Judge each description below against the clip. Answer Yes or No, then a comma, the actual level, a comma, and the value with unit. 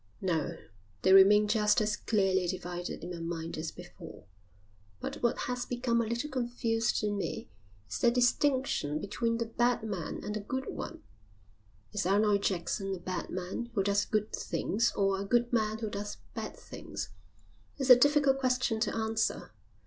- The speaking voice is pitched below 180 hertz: No, high, 215 Hz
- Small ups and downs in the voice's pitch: No, average, 3.8 semitones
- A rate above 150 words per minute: Yes, average, 170 wpm